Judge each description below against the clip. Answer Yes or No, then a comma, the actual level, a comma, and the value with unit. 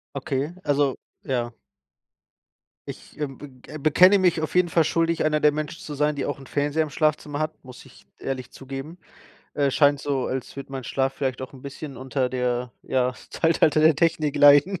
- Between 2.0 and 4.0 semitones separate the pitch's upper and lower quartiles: Yes, narrow, 2.5 semitones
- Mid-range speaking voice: Yes, medium, 145 Hz